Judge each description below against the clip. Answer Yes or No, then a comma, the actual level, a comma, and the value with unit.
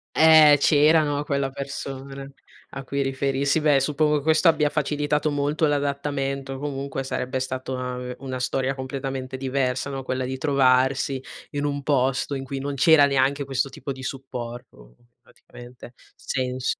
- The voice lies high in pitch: No, low, 135 Hz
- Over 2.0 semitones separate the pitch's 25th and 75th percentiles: No, narrow, 1.6 semitones